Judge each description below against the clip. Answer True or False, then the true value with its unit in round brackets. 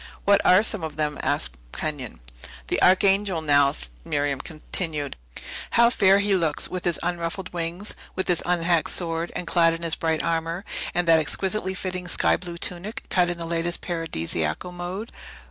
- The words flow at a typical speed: True (165 wpm)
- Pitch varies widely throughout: False (2.4 semitones)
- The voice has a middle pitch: True (170 Hz)